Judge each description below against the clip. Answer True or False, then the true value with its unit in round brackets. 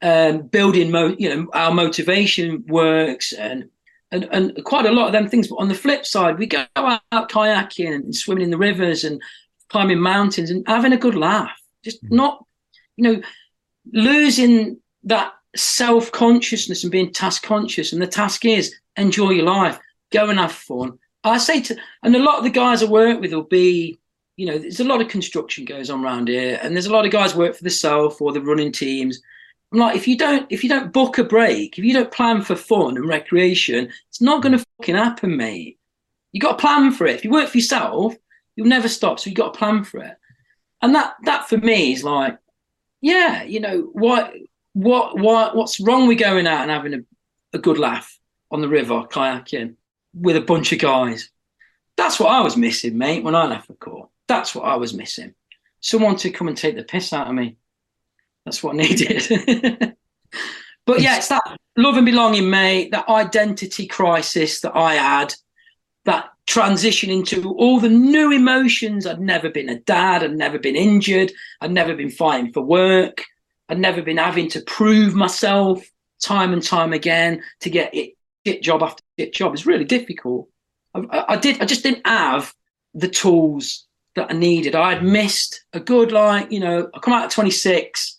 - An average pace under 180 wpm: False (200 wpm)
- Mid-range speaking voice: False (200 Hz)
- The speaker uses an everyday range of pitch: False (5.7 semitones)